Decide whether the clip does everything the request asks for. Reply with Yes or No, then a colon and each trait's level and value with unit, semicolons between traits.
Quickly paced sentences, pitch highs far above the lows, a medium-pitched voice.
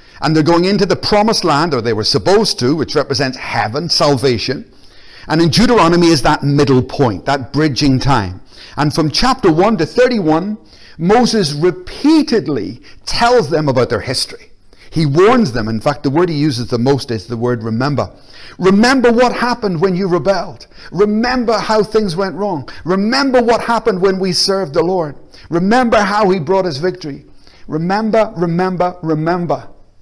No: average, 165 wpm; wide, 6.7 semitones; medium, 175 Hz